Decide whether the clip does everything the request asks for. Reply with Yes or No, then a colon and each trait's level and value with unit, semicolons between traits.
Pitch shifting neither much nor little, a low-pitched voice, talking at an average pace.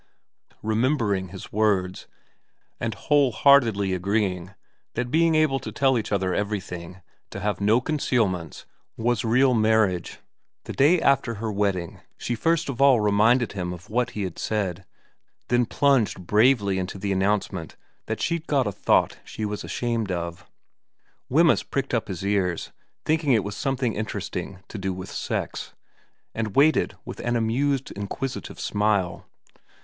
Yes: average, 4.7 semitones; low, 110 Hz; average, 155 wpm